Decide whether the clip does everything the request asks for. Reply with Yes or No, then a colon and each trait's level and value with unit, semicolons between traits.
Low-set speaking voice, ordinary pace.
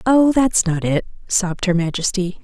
No: high, 195 Hz; average, 170 wpm